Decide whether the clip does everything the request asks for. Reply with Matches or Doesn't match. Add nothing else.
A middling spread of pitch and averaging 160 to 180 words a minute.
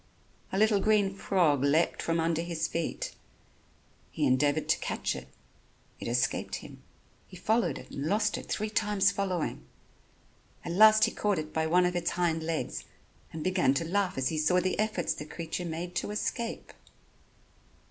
Matches